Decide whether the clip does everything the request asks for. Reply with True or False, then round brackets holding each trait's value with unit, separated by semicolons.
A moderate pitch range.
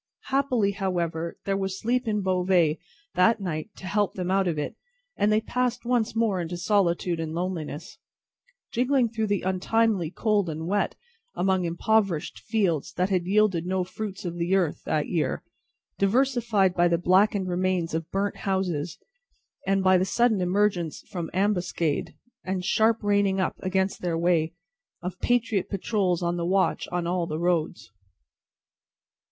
True (3.1 semitones)